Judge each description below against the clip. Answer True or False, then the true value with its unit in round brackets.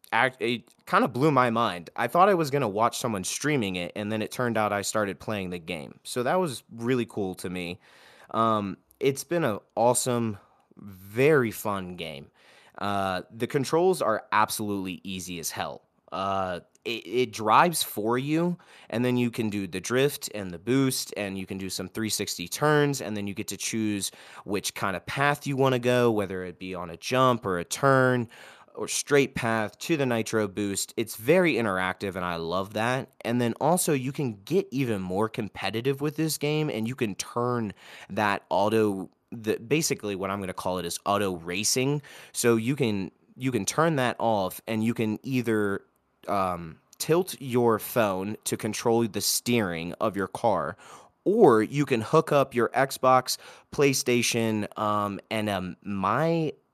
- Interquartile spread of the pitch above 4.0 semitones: True (4.8 semitones)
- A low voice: True (110 Hz)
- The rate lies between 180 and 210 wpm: True (185 wpm)